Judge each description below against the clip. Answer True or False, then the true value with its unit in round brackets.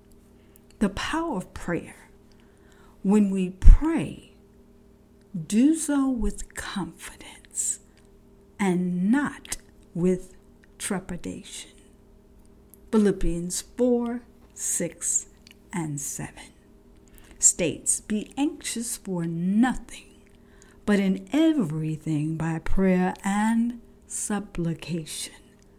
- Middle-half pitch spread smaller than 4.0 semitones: False (5.0 semitones)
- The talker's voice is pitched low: False (200 Hz)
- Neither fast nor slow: False (75 wpm)